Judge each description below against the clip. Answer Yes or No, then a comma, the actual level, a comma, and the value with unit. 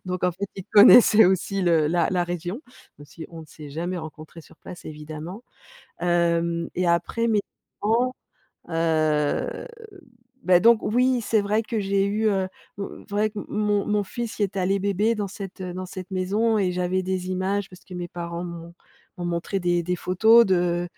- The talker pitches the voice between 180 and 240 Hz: Yes, medium, 185 Hz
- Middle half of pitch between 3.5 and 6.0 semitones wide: No, average, 3.0 semitones